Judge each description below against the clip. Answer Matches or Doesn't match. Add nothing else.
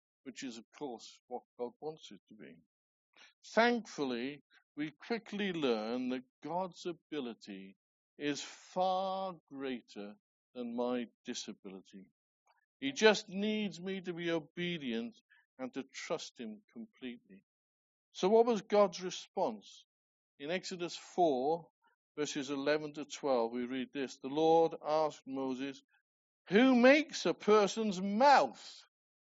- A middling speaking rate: Doesn't match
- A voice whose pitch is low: Doesn't match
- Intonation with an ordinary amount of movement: Doesn't match